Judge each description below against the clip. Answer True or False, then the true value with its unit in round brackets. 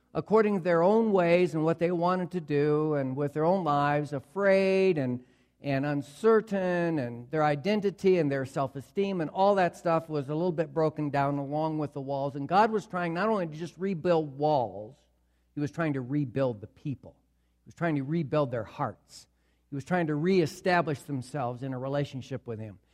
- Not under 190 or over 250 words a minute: True (200 wpm)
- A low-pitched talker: False (150 Hz)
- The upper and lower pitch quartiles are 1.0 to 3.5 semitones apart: False (4.4 semitones)